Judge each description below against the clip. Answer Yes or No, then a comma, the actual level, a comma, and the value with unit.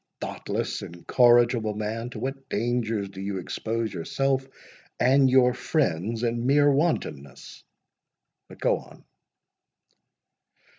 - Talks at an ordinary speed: No, slow, 100 wpm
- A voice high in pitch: No, low, 120 Hz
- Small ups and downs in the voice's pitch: No, average, 4.0 semitones